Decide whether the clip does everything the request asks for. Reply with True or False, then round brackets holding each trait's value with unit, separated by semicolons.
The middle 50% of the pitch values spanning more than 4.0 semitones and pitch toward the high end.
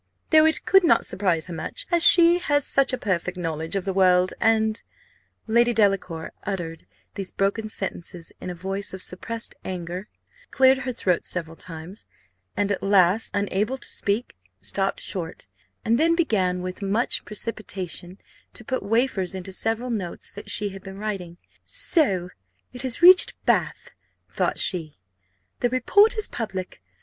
True (4.6 semitones; 200 Hz)